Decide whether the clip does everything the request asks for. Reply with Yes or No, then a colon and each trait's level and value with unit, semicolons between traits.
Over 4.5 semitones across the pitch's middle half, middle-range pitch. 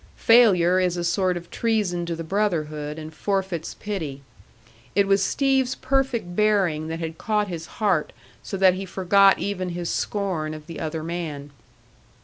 No: average, 3.8 semitones; medium, 180 Hz